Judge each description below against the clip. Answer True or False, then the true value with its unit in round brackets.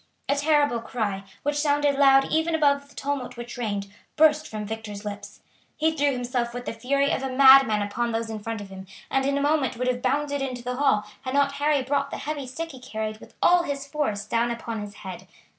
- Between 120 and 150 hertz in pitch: False (260 Hz)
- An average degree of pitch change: True (4.3 semitones)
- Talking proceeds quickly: True (225 wpm)